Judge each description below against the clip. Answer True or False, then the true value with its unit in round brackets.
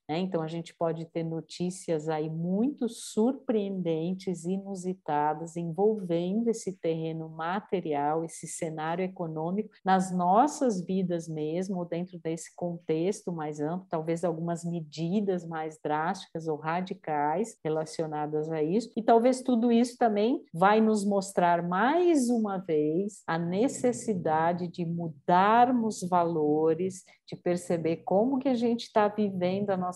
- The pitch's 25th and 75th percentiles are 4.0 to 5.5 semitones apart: True (4.3 semitones)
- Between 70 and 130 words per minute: True (125 wpm)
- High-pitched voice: False (180 Hz)